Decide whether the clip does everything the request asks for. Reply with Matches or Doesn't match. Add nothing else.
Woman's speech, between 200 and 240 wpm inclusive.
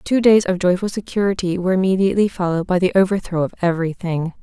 Matches